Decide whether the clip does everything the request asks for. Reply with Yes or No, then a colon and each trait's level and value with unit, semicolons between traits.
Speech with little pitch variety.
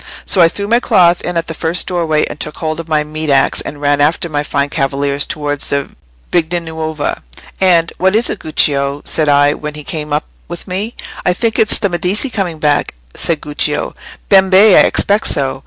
No: average, 3.6 semitones